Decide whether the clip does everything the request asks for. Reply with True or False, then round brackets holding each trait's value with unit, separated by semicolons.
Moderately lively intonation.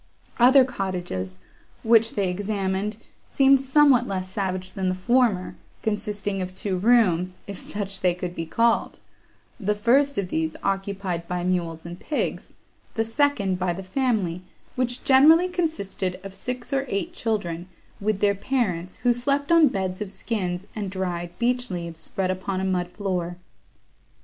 True (4.7 semitones)